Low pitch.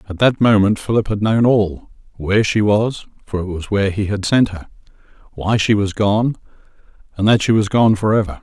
Yes: low, 105 Hz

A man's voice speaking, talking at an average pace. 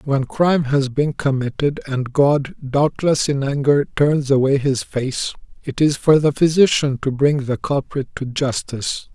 Yes: male; average, 165 wpm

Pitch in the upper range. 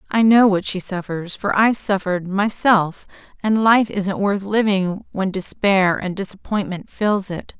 Yes: high, 195 Hz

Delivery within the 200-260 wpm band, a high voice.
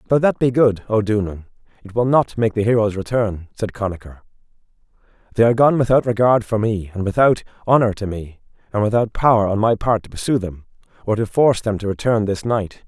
No: fast, 205 wpm; low, 110 Hz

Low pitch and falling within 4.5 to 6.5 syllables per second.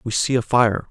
Yes: low, 115 Hz; 5.1 syllables/s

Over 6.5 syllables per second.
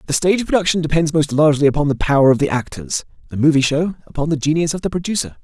Yes: 7.2 syllables/s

